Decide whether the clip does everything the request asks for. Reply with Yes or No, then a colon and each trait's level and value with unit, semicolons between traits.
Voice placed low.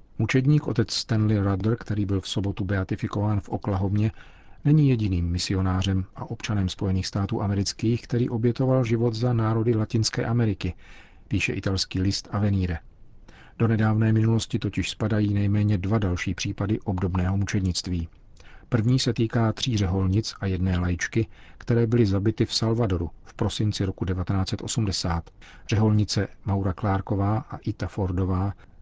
Yes: low, 105 Hz